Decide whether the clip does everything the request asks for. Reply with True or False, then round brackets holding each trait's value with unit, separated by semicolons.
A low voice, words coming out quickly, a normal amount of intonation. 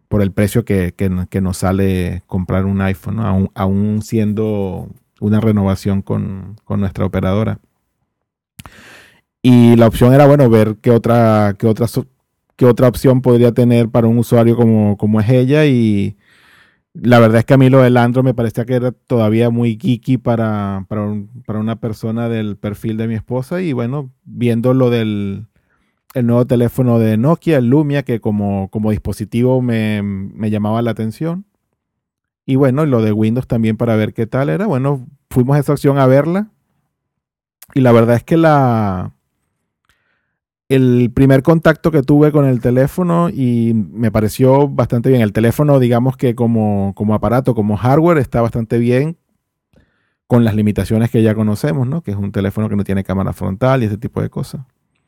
False (115 Hz; 175 wpm; 3.4 semitones)